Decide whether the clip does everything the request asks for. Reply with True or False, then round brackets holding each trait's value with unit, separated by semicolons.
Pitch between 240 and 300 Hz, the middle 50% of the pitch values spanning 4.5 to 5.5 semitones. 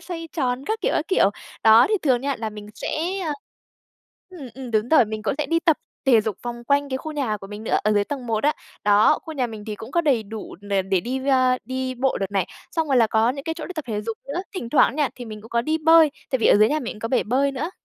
True (255 Hz; 4.8 semitones)